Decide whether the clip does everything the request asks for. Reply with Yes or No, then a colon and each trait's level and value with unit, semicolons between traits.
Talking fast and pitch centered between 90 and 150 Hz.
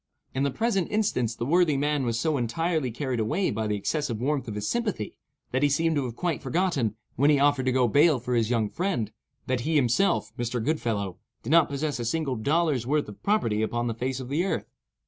Yes: fast, 225 wpm; low, 135 Hz